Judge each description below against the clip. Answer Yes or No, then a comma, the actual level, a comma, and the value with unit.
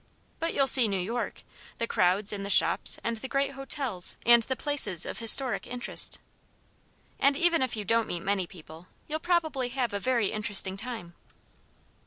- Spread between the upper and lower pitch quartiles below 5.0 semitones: No, average, 5.3 semitones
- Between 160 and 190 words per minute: Yes, average, 175 wpm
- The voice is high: Yes, high, 230 Hz